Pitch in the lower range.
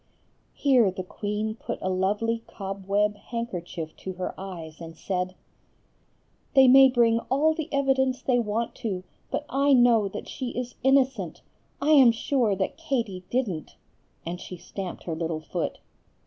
No: high, 220 Hz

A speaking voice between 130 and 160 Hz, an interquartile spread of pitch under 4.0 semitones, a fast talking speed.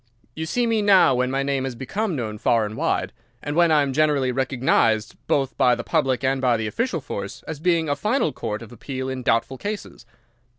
No: low, 135 Hz; average, 4.6 semitones; fast, 215 wpm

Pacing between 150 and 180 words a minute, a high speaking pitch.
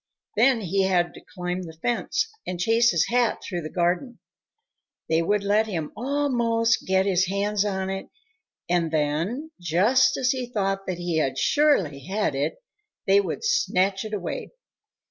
Yes: average, 160 wpm; high, 195 Hz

